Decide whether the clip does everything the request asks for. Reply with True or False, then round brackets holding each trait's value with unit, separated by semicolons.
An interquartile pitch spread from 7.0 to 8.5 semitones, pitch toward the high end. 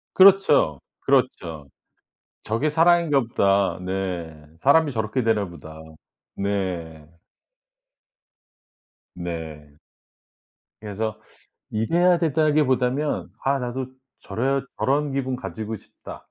False (7.4 semitones; 110 Hz)